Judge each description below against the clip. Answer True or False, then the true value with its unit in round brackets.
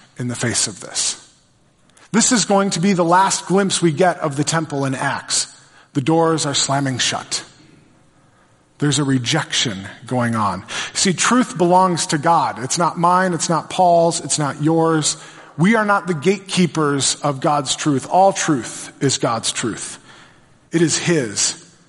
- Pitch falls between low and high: True (160 Hz)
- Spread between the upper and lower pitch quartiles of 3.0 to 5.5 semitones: True (4.0 semitones)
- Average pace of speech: True (165 wpm)